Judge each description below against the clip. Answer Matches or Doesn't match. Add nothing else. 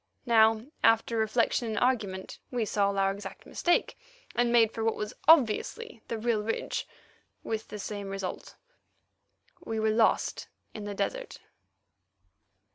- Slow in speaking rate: Matches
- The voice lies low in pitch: Doesn't match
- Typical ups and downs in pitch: Doesn't match